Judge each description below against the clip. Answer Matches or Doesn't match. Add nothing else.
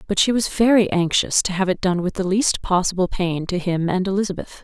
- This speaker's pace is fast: Matches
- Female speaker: Matches